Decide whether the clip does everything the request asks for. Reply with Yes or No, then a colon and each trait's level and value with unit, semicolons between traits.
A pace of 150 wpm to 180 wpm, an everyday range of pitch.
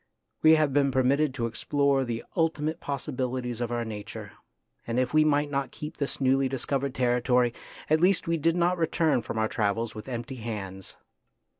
Yes: average, 175 wpm; average, 4.1 semitones